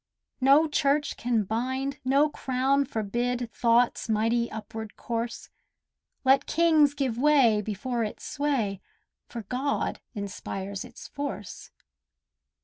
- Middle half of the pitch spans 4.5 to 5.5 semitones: No, average, 3.9 semitones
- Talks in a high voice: Yes, high, 245 Hz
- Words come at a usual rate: No, slow, 110 wpm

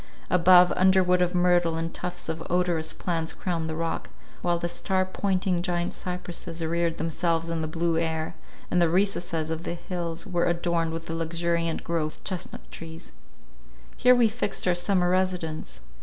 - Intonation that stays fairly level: Yes, narrow, 1.7 semitones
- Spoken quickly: No, average, 170 wpm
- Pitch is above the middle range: No, medium, 170 Hz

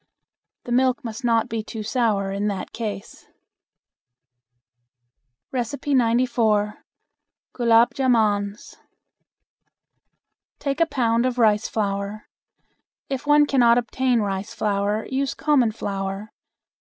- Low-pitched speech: No, high, 230 Hz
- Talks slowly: Yes, slow, 100 wpm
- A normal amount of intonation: Yes, average, 3.4 semitones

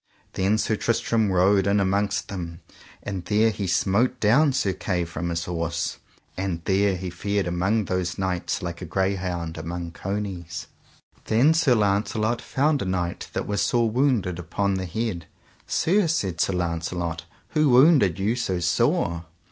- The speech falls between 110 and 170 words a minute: Yes, average, 155 wpm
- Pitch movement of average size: Yes, average, 3.8 semitones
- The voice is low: Yes, very low, 95 Hz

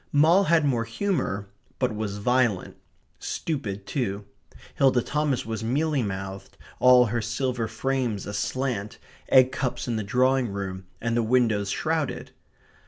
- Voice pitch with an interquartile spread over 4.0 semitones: Yes, average, 4.5 semitones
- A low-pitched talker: Yes, low, 120 Hz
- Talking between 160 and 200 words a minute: No, slow, 135 wpm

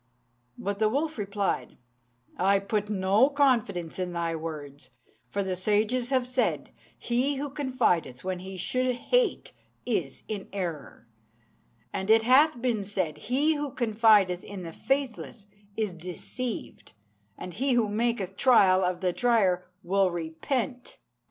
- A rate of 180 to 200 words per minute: No, average, 140 wpm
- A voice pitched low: No, high, 205 Hz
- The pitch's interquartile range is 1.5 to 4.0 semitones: No, wide, 5.4 semitones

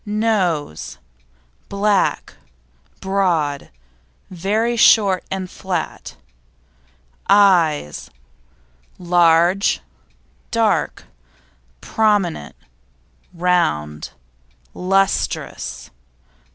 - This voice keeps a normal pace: No, slow, 45 wpm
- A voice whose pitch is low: No, medium, 185 Hz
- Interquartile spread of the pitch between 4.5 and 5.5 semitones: No, average, 3.4 semitones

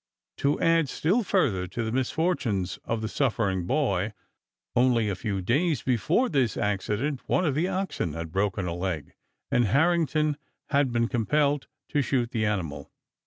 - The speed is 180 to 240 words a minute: No, average, 160 wpm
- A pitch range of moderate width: No, wide, 6.8 semitones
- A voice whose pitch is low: Yes, low, 120 Hz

